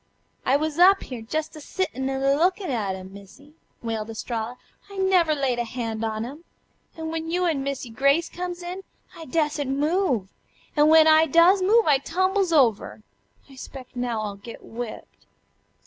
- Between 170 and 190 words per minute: Yes, average, 180 wpm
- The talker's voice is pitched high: Yes, very high, 285 Hz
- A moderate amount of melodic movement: No, wide, 5.9 semitones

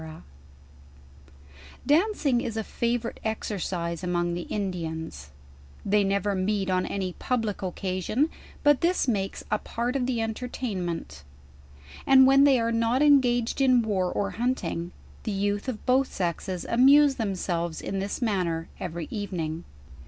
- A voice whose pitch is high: Yes, high, 205 Hz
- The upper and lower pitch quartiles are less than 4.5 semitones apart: No, wide, 5.4 semitones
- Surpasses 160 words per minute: No, slow, 135 wpm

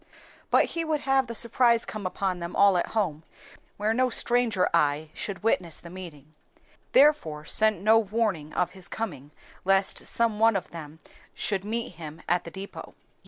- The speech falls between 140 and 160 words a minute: No, average, 170 wpm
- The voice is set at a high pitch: Yes, high, 195 Hz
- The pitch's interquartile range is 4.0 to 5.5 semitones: Yes, average, 5.1 semitones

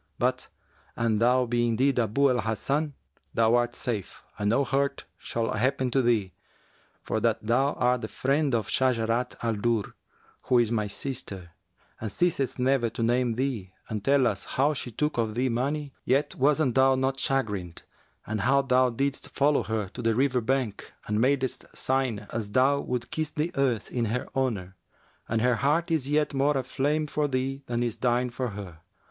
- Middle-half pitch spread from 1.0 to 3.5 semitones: Yes, average, 3.2 semitones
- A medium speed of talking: Yes, average, 180 wpm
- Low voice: Yes, low, 125 Hz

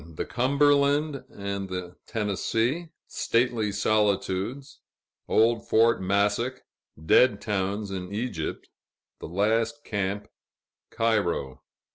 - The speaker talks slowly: Yes, slow, 90 wpm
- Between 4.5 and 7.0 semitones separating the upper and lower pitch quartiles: No, average, 3.9 semitones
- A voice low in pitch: Yes, low, 105 Hz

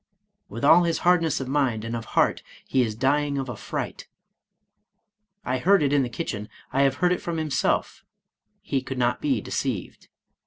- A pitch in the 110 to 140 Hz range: Yes, low, 135 Hz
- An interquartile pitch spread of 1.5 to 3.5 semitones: No, average, 4.6 semitones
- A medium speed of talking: Yes, average, 195 wpm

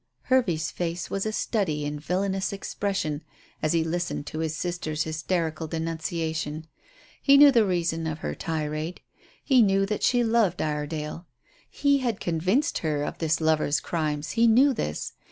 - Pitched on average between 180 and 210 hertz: No, medium, 165 Hz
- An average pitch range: Yes, average, 4.2 semitones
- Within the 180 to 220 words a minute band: No, average, 155 wpm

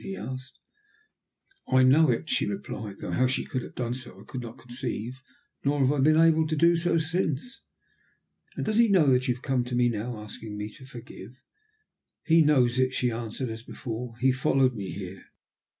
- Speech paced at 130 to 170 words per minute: No, average, 200 wpm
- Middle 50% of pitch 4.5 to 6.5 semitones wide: No, average, 3.7 semitones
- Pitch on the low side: Yes, low, 130 Hz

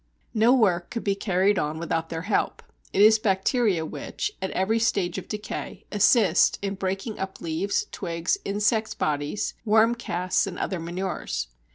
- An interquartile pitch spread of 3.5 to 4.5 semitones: Yes, average, 3.9 semitones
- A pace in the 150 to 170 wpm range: Yes, average, 160 wpm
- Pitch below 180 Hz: No, high, 195 Hz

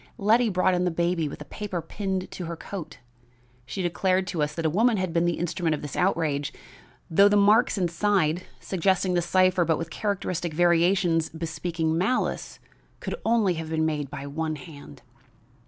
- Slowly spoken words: No, average, 180 wpm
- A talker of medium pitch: Yes, medium, 175 Hz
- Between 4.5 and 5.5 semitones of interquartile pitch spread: No, average, 3.0 semitones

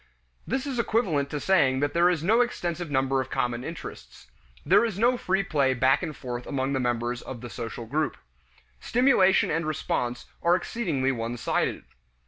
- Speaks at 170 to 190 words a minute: Yes, average, 175 wpm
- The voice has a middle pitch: Yes, medium, 145 Hz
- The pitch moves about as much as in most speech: No, wide, 6.3 semitones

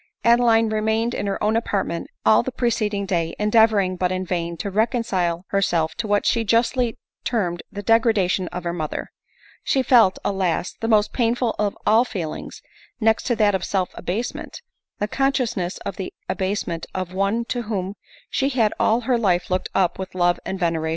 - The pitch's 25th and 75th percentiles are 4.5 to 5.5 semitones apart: No, average, 3.8 semitones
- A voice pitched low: No, high, 205 Hz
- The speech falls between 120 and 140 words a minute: No, average, 185 wpm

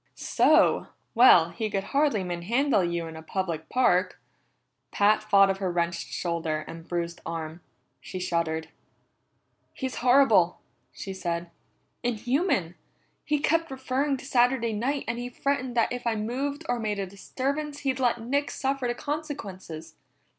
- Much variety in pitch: Yes, wide, 7.3 semitones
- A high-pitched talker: Yes, high, 220 Hz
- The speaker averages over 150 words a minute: No, average, 145 wpm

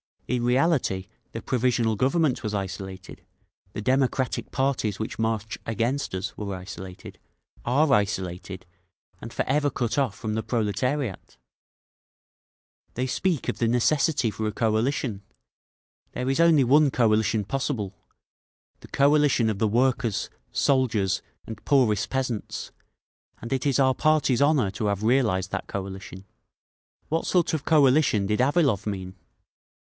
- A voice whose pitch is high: No, low, 120 Hz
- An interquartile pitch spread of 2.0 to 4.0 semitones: No, average, 4.9 semitones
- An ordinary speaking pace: No, slow, 130 wpm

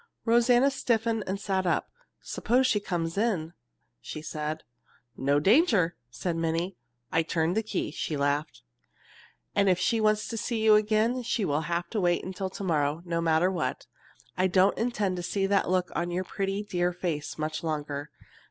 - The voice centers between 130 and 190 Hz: Yes, medium, 185 Hz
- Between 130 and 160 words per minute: No, average, 170 wpm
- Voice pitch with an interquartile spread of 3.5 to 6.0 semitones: Yes, average, 4.5 semitones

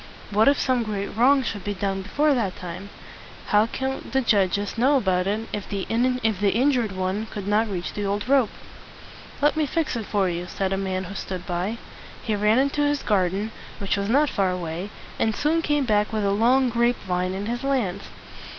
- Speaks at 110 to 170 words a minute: No, fast, 205 wpm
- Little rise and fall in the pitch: No, average, 4.6 semitones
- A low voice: No, high, 210 Hz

